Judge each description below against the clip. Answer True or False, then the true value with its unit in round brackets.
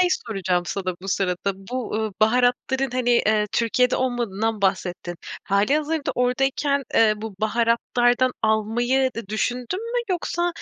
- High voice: True (235 Hz)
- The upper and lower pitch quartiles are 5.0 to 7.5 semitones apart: False (3.5 semitones)